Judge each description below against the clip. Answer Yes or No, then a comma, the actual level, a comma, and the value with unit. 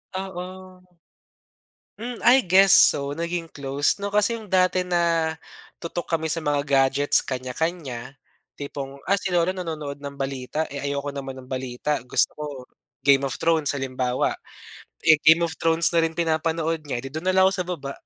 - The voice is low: No, medium, 155 Hz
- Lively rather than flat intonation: No, average, 3.8 semitones